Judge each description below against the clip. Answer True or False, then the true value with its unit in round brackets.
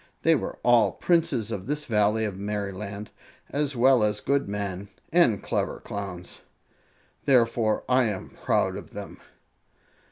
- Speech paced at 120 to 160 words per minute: True (135 wpm)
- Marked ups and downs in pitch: False (4.3 semitones)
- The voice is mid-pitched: False (110 Hz)